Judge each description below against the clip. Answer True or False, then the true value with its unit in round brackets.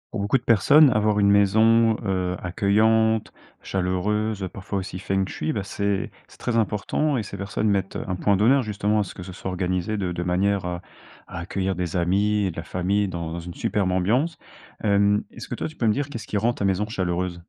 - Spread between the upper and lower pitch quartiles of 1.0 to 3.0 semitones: True (2.7 semitones)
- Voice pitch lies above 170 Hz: False (100 Hz)